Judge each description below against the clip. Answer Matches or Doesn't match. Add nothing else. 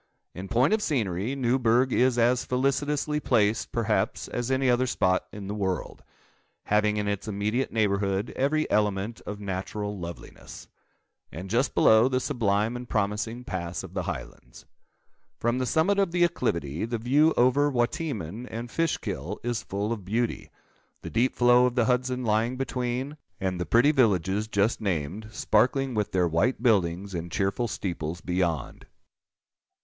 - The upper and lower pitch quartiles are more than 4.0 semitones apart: Matches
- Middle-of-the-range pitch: Doesn't match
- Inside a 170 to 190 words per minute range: Doesn't match